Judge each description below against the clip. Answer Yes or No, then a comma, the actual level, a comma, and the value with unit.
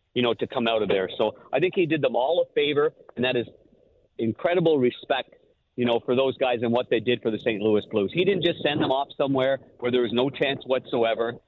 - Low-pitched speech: Yes, low, 125 Hz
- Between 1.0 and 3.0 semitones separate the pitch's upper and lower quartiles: No, average, 4.3 semitones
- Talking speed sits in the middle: No, fast, 250 wpm